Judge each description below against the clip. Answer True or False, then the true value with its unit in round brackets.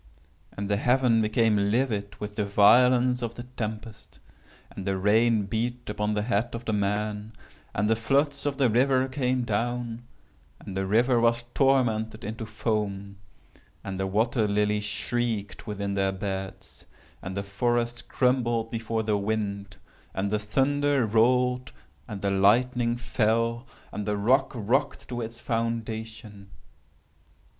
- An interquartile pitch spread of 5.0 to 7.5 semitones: False (2.9 semitones)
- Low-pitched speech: True (110 Hz)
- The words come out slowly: True (125 wpm)